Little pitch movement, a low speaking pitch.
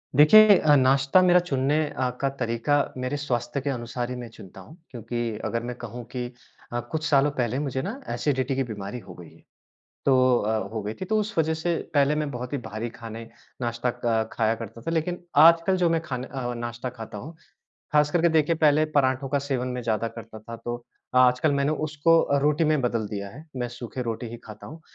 No: average, 4.1 semitones; low, 130 Hz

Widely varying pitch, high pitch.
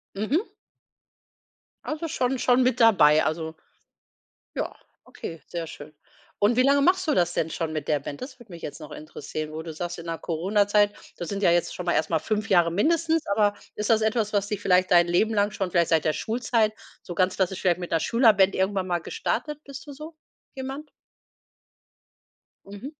Yes: wide, 6.1 semitones; high, 200 Hz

